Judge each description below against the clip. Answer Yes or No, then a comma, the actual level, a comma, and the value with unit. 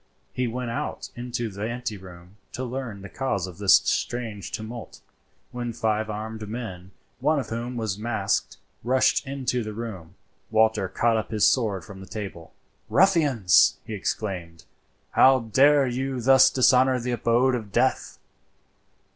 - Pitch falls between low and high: No, low, 115 Hz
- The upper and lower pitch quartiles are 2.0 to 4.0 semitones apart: Yes, average, 3.4 semitones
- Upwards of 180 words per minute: No, average, 150 wpm